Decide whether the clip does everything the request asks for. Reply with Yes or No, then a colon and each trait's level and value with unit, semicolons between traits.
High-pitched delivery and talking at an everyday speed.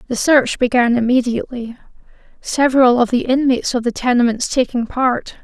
Yes: high, 245 Hz; average, 145 wpm